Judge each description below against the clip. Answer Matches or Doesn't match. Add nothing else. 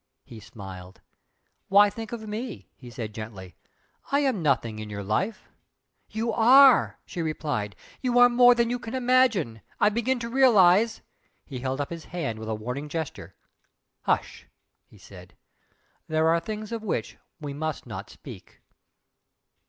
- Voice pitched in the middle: Matches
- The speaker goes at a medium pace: Matches